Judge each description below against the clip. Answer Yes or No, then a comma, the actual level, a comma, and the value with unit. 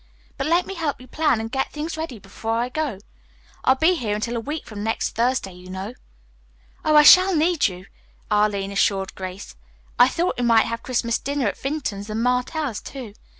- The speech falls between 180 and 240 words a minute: Yes, average, 195 wpm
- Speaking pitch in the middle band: No, high, 245 Hz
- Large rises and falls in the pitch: Yes, wide, 6.2 semitones